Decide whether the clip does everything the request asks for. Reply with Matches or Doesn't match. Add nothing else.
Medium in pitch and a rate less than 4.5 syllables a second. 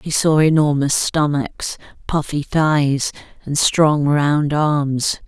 Matches